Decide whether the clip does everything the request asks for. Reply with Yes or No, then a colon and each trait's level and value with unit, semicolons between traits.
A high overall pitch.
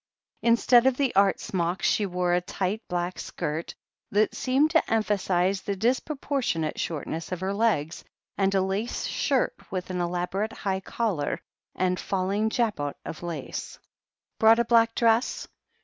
Yes: high, 195 Hz